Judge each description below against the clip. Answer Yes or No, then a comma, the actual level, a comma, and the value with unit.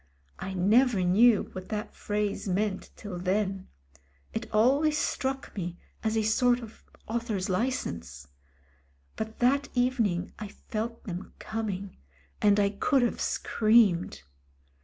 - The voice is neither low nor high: No, high, 215 Hz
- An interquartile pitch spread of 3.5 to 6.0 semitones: Yes, average, 3.9 semitones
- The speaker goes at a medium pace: No, slow, 125 wpm